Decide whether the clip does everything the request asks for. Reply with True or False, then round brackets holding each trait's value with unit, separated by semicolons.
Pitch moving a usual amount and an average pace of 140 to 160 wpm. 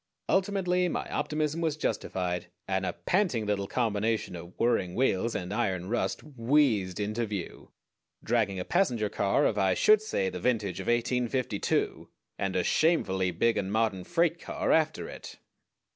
False (7.7 semitones; 155 wpm)